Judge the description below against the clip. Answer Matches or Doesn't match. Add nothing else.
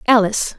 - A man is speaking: Doesn't match